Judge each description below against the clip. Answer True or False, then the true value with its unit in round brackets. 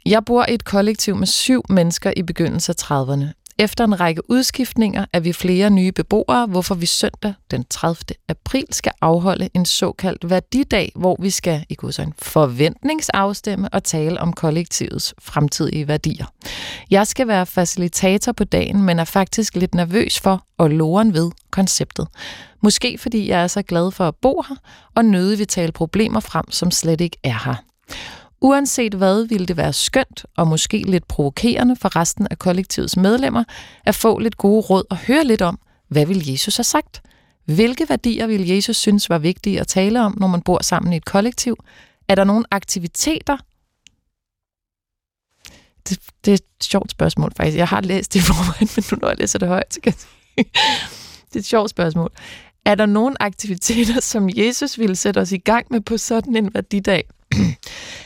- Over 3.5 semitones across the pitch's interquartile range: True (4.2 semitones)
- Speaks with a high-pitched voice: True (195 Hz)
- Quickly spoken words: False (180 wpm)